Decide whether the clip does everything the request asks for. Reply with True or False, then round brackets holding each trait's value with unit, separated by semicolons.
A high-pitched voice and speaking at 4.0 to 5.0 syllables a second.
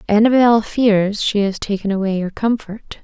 True (210 Hz; 4.5 syllables/s)